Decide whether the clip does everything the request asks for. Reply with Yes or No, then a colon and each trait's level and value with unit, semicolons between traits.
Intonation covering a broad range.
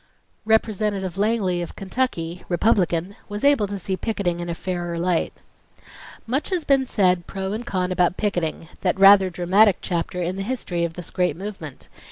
No: average, 3.2 semitones